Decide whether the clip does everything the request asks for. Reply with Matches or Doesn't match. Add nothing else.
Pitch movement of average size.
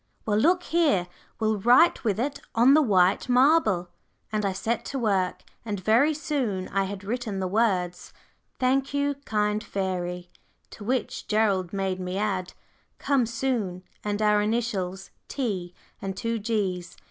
Matches